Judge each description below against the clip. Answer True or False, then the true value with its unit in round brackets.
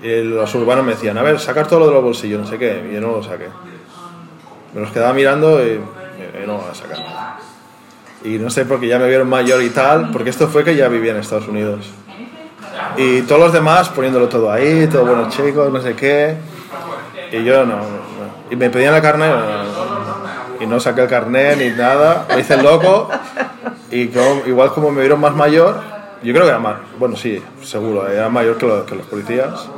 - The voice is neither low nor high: False (125 Hz)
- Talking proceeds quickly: True (220 wpm)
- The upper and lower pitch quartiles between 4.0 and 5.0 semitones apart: True (4.4 semitones)